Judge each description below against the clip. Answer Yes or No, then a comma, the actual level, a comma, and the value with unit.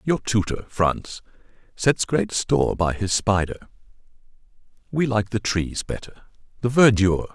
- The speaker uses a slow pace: Yes, slow, 125 wpm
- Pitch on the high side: No, low, 110 Hz